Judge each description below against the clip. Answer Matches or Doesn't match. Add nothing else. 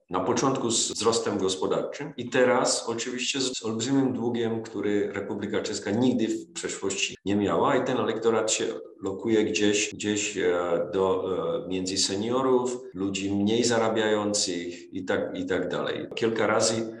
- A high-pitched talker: Doesn't match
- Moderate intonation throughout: Matches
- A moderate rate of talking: Matches